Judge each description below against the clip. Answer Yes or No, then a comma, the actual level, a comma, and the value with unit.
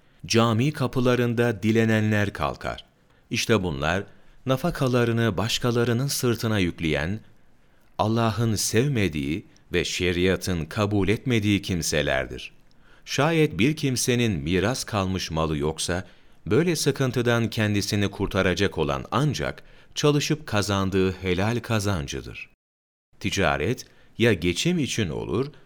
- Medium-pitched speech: No, low, 110 Hz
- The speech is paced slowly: Yes, slow, 90 wpm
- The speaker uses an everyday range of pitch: Yes, average, 4.9 semitones